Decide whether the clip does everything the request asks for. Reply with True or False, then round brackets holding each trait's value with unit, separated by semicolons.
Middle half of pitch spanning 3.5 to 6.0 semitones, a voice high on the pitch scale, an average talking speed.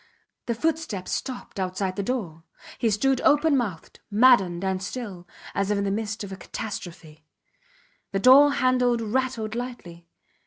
True (5.0 semitones; 215 Hz; 145 wpm)